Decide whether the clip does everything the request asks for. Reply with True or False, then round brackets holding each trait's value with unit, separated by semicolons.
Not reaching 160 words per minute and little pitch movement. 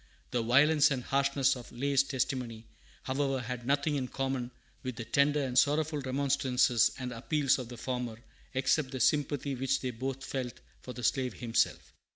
False (170 wpm; 2.1 semitones)